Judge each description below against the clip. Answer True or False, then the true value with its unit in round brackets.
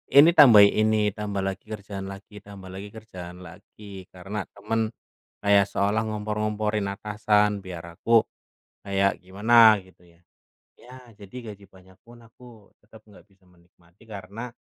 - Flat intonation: True (2.0 semitones)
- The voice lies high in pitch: False (100 Hz)